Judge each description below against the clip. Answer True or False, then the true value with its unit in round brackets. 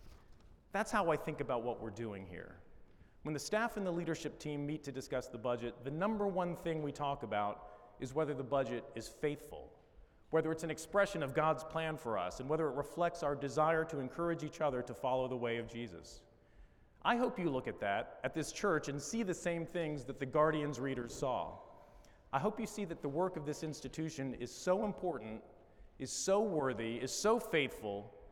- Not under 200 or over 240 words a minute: True (205 wpm)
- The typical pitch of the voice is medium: True (145 Hz)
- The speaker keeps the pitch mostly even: False (5.0 semitones)